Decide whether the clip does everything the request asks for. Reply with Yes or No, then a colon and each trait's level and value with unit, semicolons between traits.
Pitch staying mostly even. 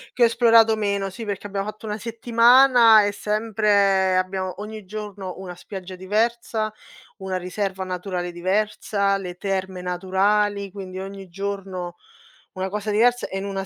Yes: narrow, 2.2 semitones